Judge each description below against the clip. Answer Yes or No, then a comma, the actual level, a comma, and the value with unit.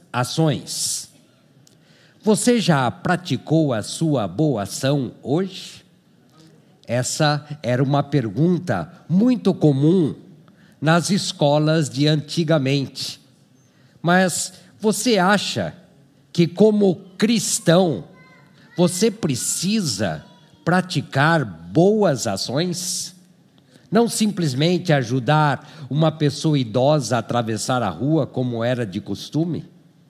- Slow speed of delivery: Yes, slow, 90 wpm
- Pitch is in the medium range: Yes, medium, 155 Hz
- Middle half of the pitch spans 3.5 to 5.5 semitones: Yes, average, 4.5 semitones